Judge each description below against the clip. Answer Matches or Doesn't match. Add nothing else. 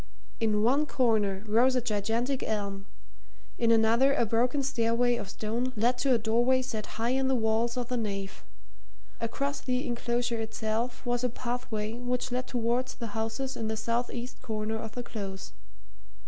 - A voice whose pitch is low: Doesn't match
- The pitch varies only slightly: Matches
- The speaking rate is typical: Matches